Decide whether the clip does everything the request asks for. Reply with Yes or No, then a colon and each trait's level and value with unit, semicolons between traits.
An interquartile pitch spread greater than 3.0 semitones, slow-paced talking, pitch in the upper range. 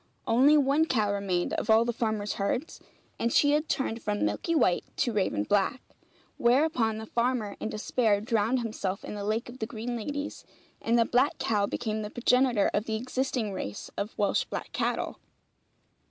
No: average, 3.4 semitones; average, 180 wpm; high, 225 Hz